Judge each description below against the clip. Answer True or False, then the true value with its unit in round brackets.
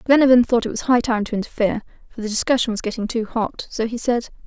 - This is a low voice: False (230 Hz)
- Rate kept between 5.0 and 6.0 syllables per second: False (6.6 syllables/s)